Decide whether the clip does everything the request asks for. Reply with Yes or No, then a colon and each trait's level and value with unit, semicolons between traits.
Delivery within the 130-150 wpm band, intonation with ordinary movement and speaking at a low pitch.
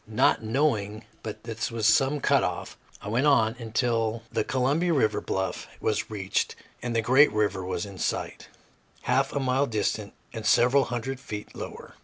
No: average, 170 wpm; average, 3.4 semitones; low, 115 Hz